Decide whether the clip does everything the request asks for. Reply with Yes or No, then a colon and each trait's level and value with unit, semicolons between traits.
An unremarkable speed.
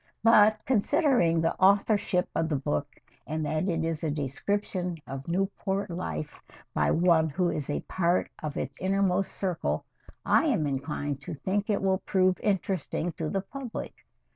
Yes: average, 160 wpm